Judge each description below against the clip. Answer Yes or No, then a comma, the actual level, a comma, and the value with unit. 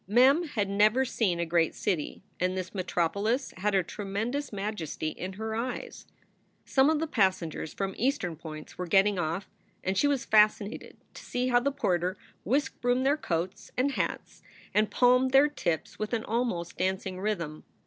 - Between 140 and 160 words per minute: No, average, 185 wpm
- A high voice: Yes, high, 205 Hz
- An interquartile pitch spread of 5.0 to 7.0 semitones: Yes, wide, 5.5 semitones